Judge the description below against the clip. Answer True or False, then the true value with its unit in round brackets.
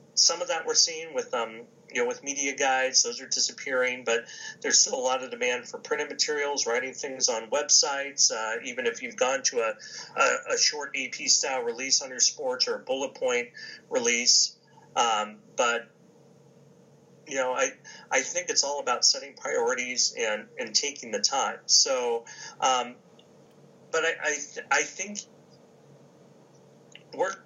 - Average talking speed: True (160 wpm)